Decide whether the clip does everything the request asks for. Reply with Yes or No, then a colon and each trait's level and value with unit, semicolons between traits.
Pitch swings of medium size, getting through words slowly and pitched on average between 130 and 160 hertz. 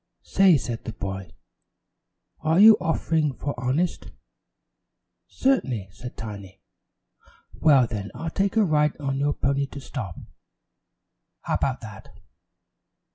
No: wide, 6.2 semitones; slow, 120 wpm; medium, 140 Hz